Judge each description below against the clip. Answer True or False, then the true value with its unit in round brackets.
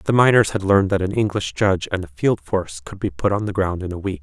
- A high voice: False (95 Hz)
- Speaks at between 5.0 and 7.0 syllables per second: True (6.2 syllables/s)